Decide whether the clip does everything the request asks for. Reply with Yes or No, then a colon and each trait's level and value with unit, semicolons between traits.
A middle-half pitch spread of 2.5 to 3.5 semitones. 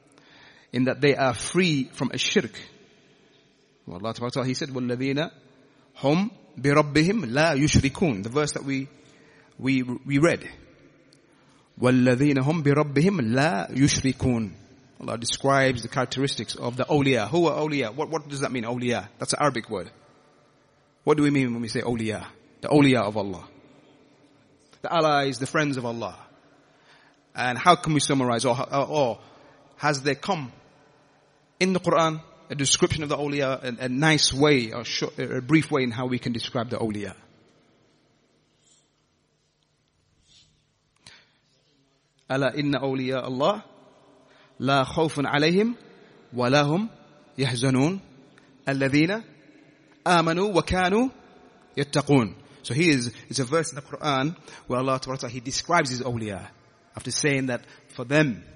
Yes: average, 2.8 semitones